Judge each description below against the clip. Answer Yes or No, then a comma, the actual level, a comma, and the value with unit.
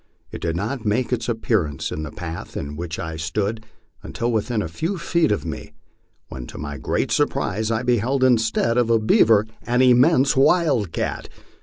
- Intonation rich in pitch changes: Yes, wide, 6.6 semitones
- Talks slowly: No, average, 175 wpm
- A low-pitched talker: Yes, low, 110 Hz